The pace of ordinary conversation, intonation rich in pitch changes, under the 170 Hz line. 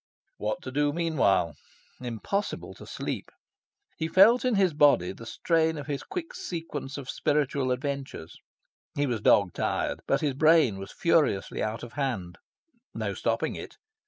Yes: average, 155 wpm; wide, 5.9 semitones; medium, 140 Hz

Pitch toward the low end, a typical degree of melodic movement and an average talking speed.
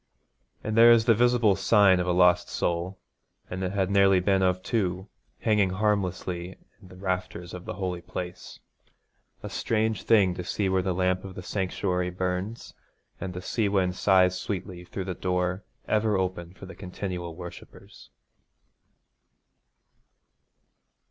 No: very low, 95 Hz; narrow, 1.8 semitones; average, 150 wpm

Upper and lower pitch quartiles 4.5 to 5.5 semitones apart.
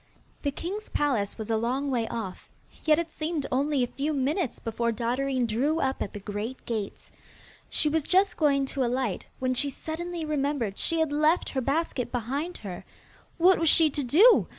Yes: average, 4.9 semitones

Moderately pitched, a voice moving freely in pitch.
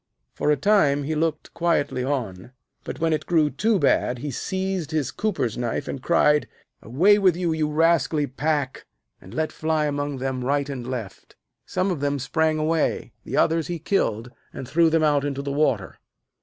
No: medium, 150 Hz; average, 3.4 semitones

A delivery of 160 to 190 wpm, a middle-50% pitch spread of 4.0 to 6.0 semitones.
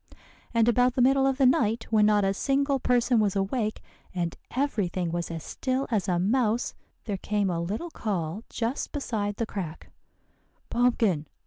Yes: average, 175 wpm; average, 4.4 semitones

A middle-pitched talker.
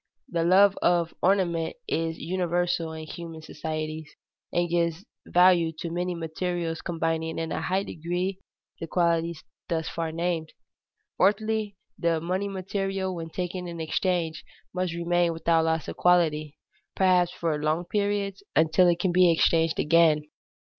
Yes: medium, 170 Hz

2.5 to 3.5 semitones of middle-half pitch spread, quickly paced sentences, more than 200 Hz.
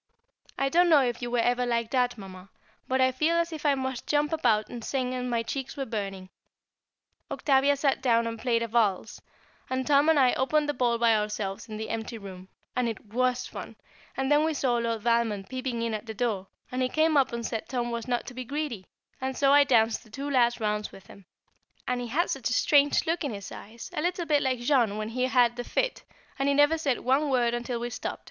Yes: average, 3.1 semitones; fast, 235 wpm; high, 245 Hz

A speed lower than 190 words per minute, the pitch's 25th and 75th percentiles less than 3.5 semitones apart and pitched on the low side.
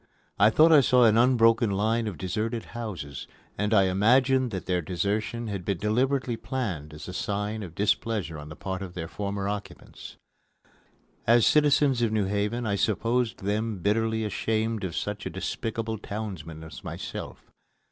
Yes: average, 165 wpm; average, 3.1 semitones; low, 105 Hz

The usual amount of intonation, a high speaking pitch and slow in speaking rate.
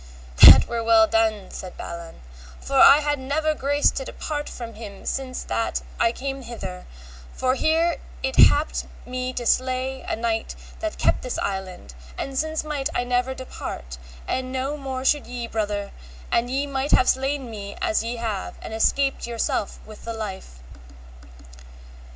No: average, 3.6 semitones; very high, 255 Hz; average, 165 wpm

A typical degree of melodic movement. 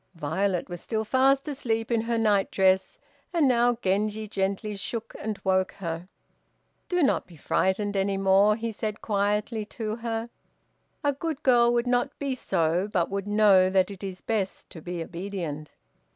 Yes: average, 3.5 semitones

